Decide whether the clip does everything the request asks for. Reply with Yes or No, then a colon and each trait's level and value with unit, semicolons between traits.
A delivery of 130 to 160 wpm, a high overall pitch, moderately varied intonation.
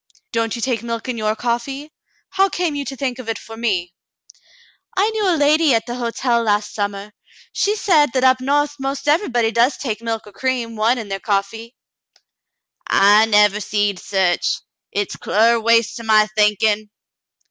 No: average, 180 wpm; high, 230 Hz; average, 4.2 semitones